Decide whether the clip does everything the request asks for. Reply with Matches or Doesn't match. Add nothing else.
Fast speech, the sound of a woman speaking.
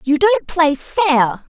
Doesn't match